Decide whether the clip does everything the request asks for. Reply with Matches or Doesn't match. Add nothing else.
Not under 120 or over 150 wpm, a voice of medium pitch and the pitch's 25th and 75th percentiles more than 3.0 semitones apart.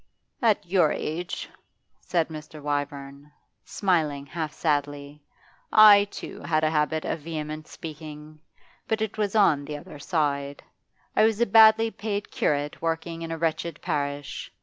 Matches